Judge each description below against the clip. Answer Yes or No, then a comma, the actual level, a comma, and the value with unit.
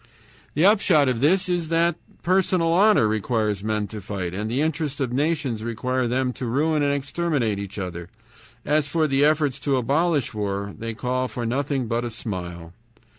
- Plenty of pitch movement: Yes, wide, 6.0 semitones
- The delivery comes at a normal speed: Yes, average, 175 wpm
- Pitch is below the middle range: Yes, low, 130 Hz